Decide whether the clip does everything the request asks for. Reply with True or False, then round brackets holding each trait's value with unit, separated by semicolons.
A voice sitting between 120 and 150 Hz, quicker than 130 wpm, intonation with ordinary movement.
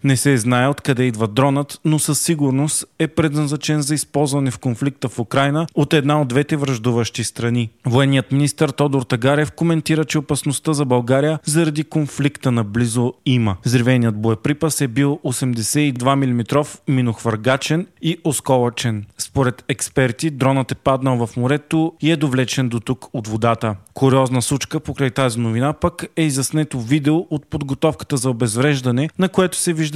True (140 Hz; 155 wpm; 3.3 semitones)